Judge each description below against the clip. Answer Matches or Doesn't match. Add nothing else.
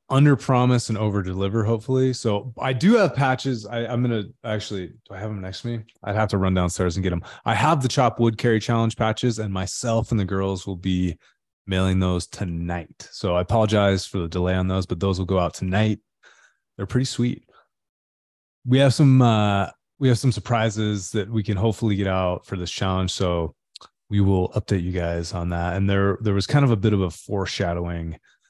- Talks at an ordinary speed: Doesn't match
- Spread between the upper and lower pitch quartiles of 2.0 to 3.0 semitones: Doesn't match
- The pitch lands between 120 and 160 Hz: Doesn't match